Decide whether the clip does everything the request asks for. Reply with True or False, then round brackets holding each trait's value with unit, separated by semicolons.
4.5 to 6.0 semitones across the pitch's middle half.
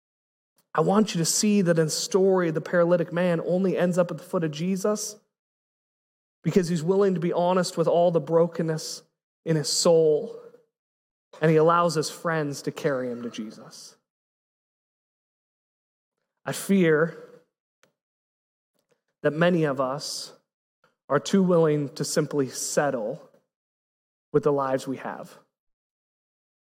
False (3.5 semitones)